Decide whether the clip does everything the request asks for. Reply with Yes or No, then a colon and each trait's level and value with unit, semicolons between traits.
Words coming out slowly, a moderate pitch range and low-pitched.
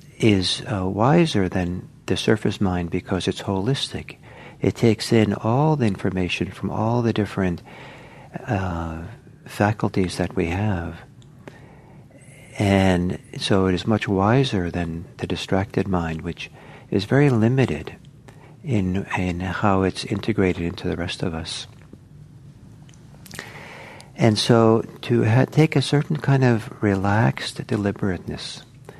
No: slow, 125 wpm; wide, 6.3 semitones; low, 110 Hz